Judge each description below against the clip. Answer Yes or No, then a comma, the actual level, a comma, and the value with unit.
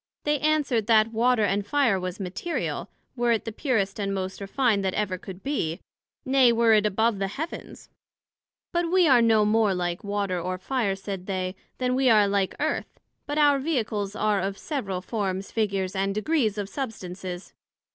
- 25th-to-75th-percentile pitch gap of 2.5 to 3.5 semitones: No, average, 4.5 semitones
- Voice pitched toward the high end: Yes, high, 210 Hz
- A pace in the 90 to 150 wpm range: No, average, 175 wpm